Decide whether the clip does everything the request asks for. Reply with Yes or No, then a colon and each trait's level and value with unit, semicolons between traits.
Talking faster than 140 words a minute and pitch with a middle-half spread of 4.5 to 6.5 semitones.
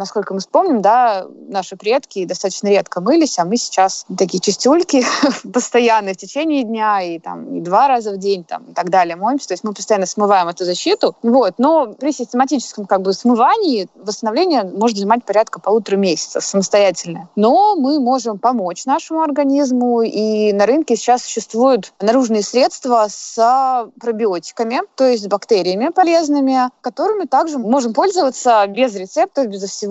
Yes: fast, 160 wpm; average, 5.0 semitones